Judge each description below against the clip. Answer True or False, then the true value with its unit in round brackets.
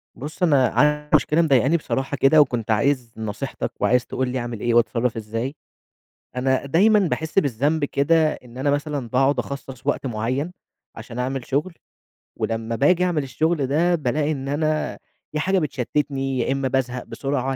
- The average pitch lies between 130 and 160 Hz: True (135 Hz)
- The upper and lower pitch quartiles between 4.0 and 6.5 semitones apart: False (3.3 semitones)